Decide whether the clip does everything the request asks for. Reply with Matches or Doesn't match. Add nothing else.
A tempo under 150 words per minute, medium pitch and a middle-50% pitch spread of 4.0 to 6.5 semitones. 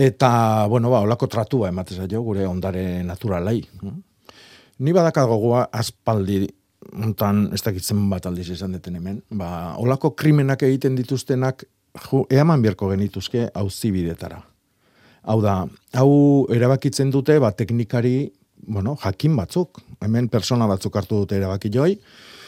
Doesn't match